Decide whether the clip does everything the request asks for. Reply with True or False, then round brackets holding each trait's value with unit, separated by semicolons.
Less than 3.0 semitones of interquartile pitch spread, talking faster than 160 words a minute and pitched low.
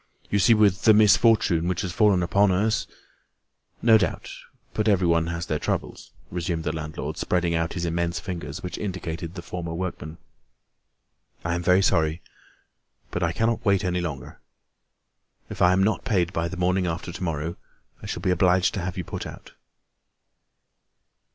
True (2.4 semitones; 170 wpm; 90 Hz)